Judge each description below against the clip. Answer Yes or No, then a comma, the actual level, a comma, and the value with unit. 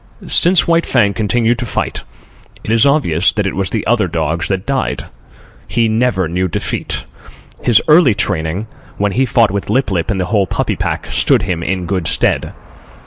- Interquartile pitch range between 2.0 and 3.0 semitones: No, average, 4.7 semitones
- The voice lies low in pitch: Yes, low, 100 Hz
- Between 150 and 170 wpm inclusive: No, average, 185 wpm